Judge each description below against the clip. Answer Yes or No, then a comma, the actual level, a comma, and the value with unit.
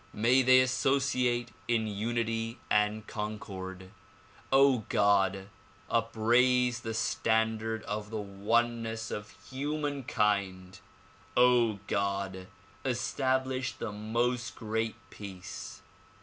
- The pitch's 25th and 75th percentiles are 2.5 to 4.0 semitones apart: Yes, average, 3.0 semitones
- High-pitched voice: No, low, 115 Hz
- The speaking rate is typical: No, slow, 80 wpm